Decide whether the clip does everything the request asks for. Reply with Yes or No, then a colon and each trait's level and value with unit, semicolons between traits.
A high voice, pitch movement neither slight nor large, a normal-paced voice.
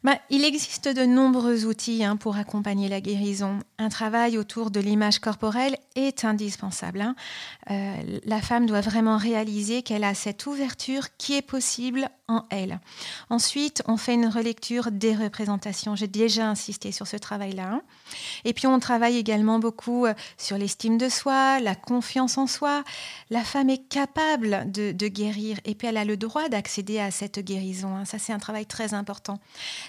Yes: high, 220 Hz; average, 3.2 semitones; average, 175 wpm